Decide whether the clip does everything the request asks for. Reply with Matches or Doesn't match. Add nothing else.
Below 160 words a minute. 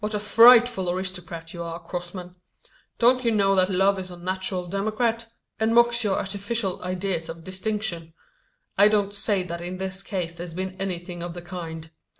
Doesn't match